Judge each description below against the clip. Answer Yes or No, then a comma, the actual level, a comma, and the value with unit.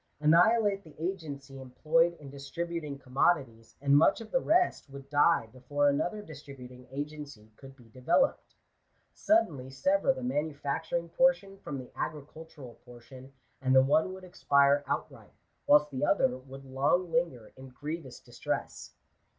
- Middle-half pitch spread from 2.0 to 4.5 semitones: Yes, average, 4.2 semitones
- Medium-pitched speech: Yes, medium, 145 Hz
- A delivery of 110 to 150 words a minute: Yes, average, 140 wpm